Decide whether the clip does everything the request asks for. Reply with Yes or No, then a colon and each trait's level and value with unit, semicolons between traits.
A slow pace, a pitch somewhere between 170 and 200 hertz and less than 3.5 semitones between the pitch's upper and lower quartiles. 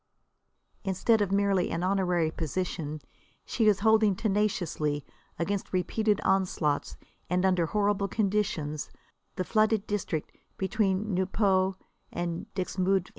Yes: slow, 110 wpm; high, 190 Hz; average, 2.7 semitones